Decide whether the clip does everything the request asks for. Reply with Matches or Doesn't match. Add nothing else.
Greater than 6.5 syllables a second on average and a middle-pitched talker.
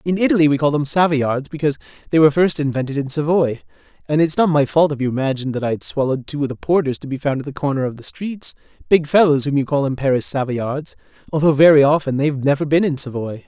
Matches